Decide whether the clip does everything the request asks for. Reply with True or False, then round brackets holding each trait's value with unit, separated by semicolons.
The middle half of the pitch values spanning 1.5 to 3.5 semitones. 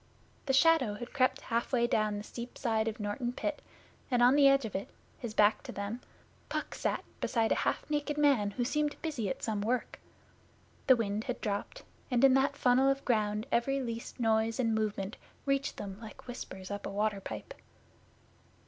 False (4.0 semitones)